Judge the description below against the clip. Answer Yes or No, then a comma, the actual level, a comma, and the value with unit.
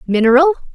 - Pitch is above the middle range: Yes, very high, 275 Hz